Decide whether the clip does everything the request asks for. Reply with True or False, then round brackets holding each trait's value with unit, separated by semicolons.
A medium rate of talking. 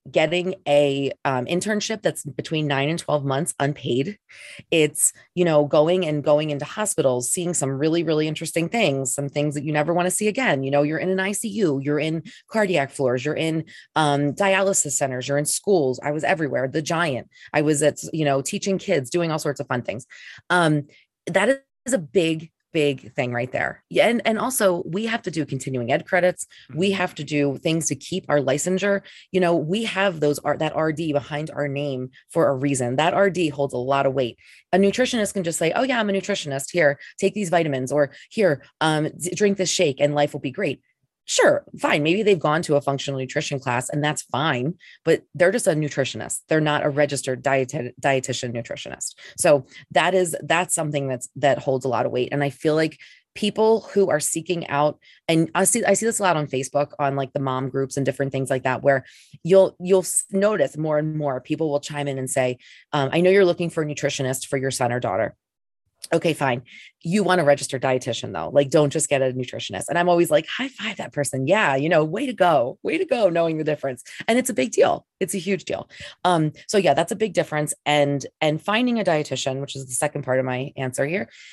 False (220 wpm)